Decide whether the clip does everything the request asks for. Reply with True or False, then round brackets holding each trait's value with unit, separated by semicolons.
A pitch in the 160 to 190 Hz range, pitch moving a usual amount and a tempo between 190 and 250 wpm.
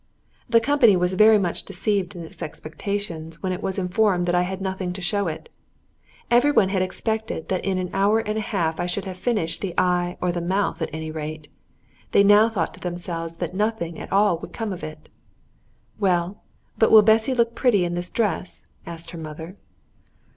True (185 Hz; 3.3 semitones; 200 wpm)